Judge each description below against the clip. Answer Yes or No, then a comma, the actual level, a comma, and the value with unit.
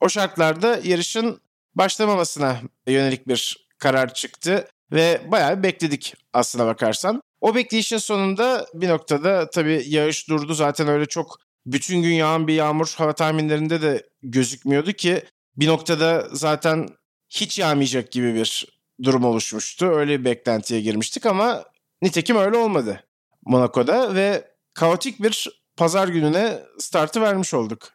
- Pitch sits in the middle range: Yes, medium, 160 Hz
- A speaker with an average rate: Yes, average, 130 wpm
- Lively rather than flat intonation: Yes, wide, 6.0 semitones